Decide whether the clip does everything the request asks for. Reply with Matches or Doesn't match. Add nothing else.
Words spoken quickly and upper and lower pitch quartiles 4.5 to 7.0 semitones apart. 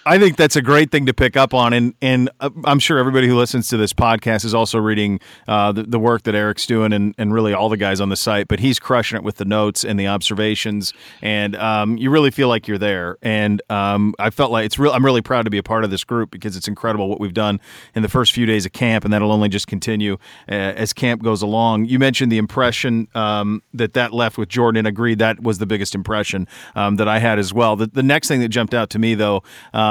Doesn't match